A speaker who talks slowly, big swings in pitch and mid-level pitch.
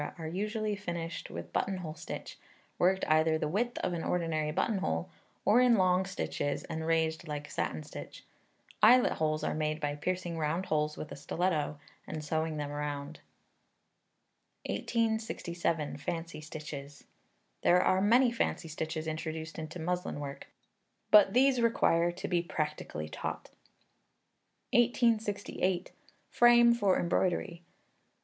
No: slow, 130 wpm; average, 4.1 semitones; medium, 170 Hz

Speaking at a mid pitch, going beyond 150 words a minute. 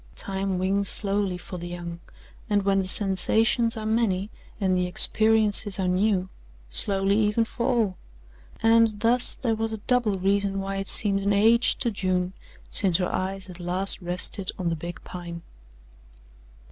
No: high, 195 Hz; average, 160 wpm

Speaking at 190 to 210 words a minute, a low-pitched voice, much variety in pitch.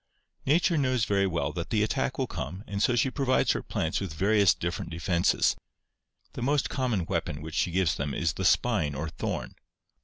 Yes: average, 195 wpm; very low, 95 Hz; wide, 6.5 semitones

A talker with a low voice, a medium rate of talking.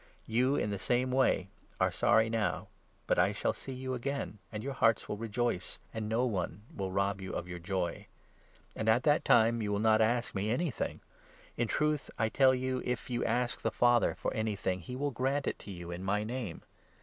No: low, 115 Hz; fast, 215 wpm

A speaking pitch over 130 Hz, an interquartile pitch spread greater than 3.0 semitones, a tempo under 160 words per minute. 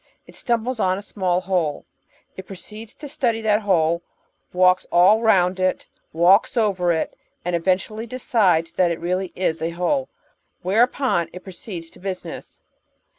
Yes: medium, 185 Hz; average, 3.8 semitones; average, 150 wpm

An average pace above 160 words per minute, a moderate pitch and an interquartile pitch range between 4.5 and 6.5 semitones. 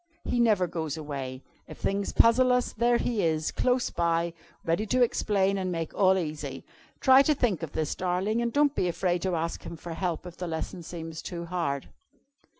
Yes: average, 195 wpm; medium, 180 Hz; average, 5.0 semitones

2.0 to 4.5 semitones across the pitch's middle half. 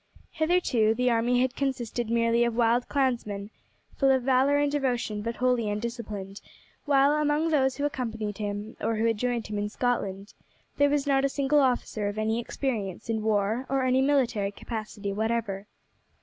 Yes: average, 3.8 semitones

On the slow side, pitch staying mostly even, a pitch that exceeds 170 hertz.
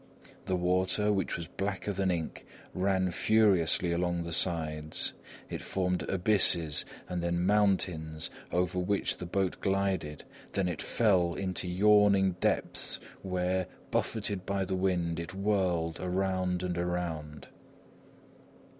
No: slow, 125 wpm; narrow, 2.0 semitones; very low, 90 Hz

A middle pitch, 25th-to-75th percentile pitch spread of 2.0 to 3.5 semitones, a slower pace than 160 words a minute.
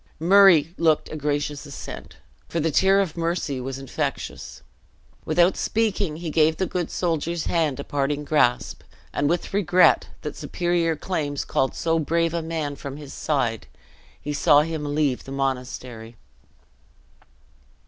Yes: medium, 155 Hz; average, 3.0 semitones; average, 145 wpm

